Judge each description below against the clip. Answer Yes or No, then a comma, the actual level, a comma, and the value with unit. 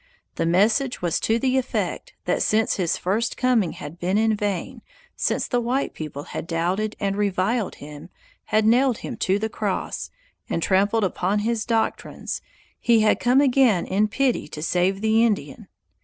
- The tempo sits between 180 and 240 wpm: No, average, 170 wpm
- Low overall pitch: No, high, 215 Hz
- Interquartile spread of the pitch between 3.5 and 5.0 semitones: Yes, average, 4.0 semitones